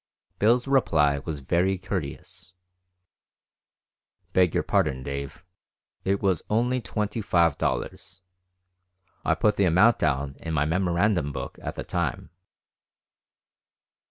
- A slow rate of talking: Yes, slow, 115 wpm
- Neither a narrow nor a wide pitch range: No, wide, 5.9 semitones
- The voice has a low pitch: Yes, very low, 90 Hz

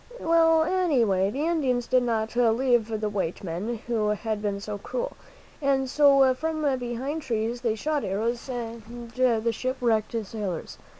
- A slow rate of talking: No, average, 160 wpm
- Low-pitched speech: No, high, 240 Hz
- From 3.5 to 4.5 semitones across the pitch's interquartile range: Yes, average, 3.9 semitones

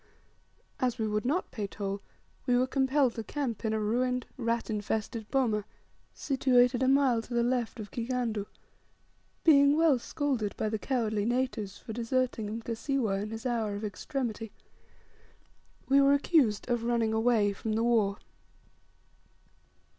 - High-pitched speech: Yes, high, 235 Hz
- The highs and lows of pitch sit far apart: No, average, 3.0 semitones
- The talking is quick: No, average, 145 wpm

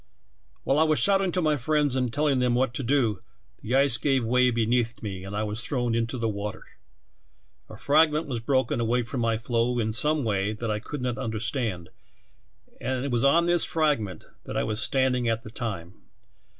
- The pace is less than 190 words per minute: No, average, 200 wpm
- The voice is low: Yes, low, 120 Hz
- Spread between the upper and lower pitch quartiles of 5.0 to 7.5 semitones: No, average, 3.7 semitones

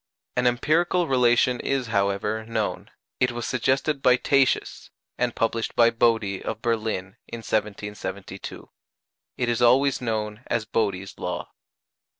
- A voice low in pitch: Yes, low, 115 Hz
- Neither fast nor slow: No, slow, 130 wpm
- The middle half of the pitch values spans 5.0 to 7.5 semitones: No, average, 2.8 semitones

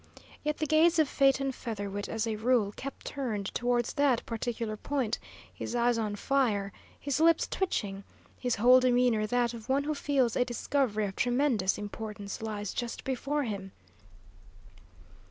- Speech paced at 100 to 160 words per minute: Yes, average, 155 wpm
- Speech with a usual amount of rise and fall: Yes, average, 4.3 semitones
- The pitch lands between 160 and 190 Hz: No, high, 240 Hz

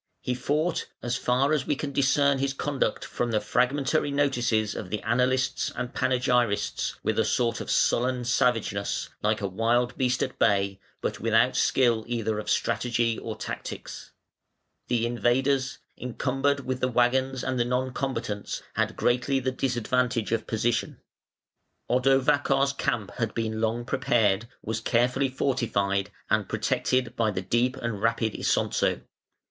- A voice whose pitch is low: Yes, low, 125 Hz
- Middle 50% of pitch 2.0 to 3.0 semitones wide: Yes, average, 2.7 semitones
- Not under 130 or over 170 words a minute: Yes, average, 145 wpm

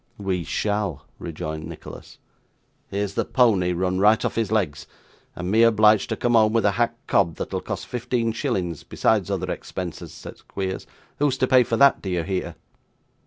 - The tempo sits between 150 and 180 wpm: Yes, average, 175 wpm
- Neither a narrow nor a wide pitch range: Yes, average, 4.2 semitones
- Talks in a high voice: No, low, 100 Hz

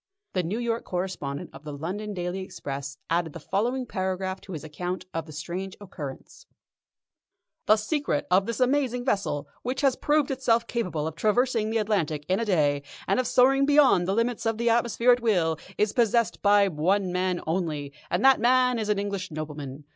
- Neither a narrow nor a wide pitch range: No, wide, 6.2 semitones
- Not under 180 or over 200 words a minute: Yes, average, 185 wpm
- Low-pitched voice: No, high, 195 Hz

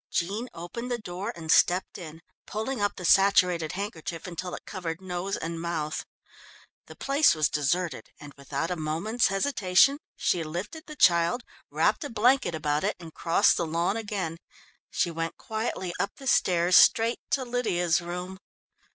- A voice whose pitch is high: No, medium, 180 Hz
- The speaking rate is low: No, average, 160 wpm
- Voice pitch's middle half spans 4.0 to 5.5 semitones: Yes, average, 4.4 semitones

